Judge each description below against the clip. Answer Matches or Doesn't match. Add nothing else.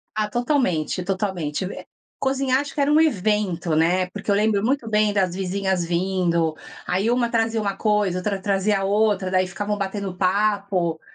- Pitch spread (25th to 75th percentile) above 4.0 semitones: Doesn't match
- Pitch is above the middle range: Matches